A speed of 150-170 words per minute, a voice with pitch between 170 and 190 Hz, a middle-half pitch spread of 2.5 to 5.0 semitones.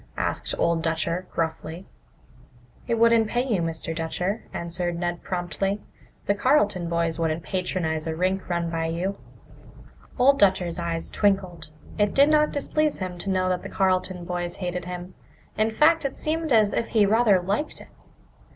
Yes: average, 160 wpm; medium, 185 Hz; average, 4.0 semitones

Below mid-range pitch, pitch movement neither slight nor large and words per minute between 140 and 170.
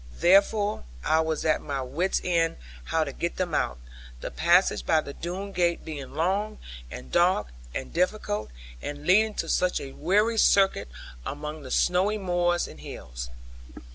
No: medium, 175 Hz; average, 4.3 semitones; average, 160 wpm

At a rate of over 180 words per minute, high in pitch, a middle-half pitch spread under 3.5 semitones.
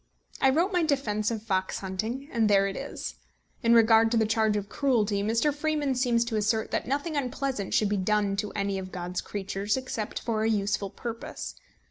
No: average, 195 wpm; high, 220 Hz; average, 4.0 semitones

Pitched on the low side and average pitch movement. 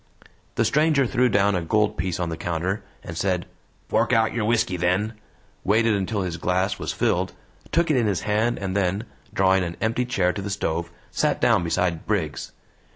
Yes: low, 100 Hz; average, 3.8 semitones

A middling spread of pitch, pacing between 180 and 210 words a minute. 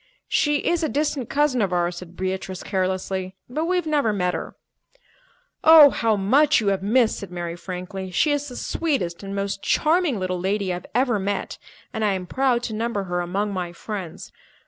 No: wide, 6.4 semitones; average, 190 wpm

